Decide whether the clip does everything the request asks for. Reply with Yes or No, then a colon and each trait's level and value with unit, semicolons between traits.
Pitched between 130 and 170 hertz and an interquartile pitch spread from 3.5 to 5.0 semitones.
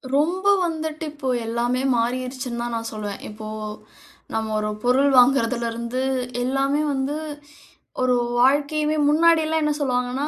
No: very high, 255 Hz; average, 4.0 semitones